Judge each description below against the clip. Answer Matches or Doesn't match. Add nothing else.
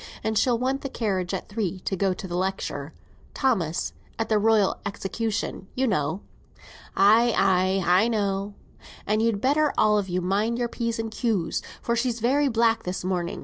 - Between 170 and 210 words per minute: Matches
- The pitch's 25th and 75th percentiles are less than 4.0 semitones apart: Matches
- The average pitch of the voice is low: Doesn't match